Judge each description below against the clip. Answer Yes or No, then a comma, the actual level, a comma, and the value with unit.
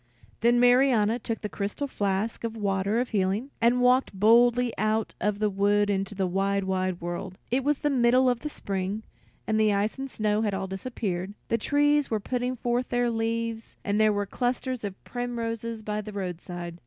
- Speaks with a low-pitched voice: No, high, 220 Hz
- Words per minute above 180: Yes, average, 190 wpm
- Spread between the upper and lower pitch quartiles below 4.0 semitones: Yes, average, 3.5 semitones